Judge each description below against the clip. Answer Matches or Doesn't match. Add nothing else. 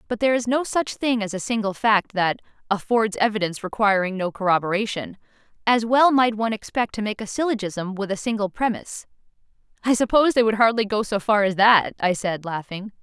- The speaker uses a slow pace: Doesn't match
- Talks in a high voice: Matches